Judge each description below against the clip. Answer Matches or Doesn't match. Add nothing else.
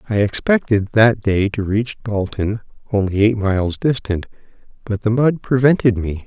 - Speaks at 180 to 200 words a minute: Doesn't match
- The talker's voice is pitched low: Matches